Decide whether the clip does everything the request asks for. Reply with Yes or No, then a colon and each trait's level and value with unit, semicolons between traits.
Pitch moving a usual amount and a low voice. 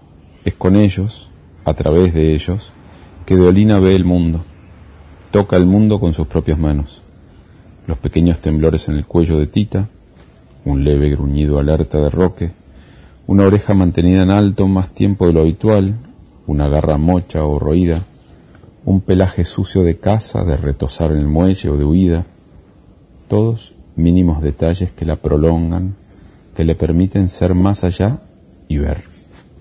Yes: average, 3.5 semitones; very low, 85 Hz